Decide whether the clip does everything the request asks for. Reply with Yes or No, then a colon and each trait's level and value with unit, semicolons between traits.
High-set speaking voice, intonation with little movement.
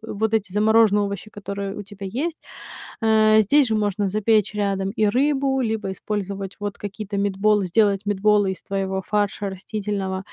Yes: high, 205 Hz; narrow, 1.7 semitones